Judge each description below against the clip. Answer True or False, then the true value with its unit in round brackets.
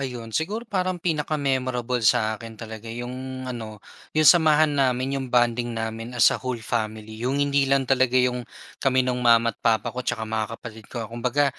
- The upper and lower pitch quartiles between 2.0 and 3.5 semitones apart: True (2.9 semitones)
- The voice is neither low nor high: False (125 Hz)